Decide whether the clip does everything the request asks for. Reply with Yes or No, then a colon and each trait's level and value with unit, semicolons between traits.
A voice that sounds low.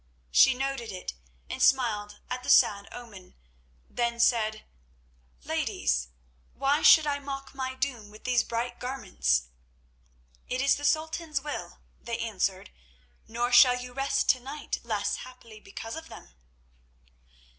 No: high, 245 Hz